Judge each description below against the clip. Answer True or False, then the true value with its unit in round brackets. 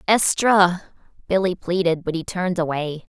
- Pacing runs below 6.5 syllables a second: True (4.9 syllables/s)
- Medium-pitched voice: True (180 Hz)